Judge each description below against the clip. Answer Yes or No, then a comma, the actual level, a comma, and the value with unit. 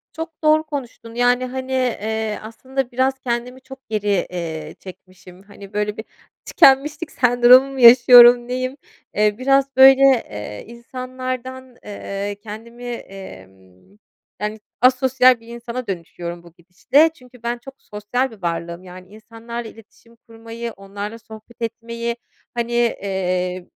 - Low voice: No, high, 235 Hz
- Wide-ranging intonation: No, average, 4.0 semitones